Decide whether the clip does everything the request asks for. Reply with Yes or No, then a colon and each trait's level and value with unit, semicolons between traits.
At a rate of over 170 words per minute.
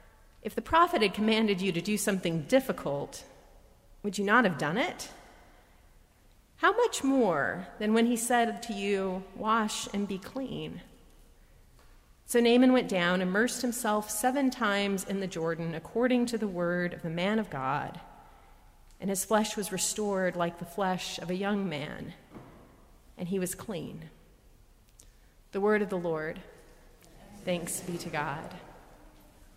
No: average, 150 wpm